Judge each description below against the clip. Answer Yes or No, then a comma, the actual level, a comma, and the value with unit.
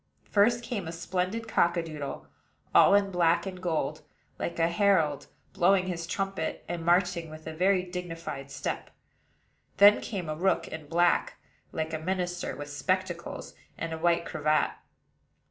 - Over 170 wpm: No, average, 150 wpm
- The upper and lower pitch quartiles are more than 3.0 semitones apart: No, average, 2.7 semitones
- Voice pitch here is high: No, medium, 175 Hz